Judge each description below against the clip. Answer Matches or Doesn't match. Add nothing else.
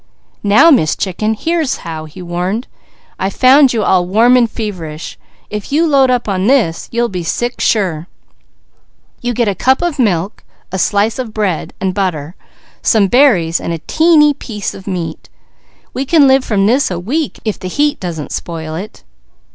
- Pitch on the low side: Doesn't match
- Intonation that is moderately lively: Doesn't match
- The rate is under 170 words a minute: Doesn't match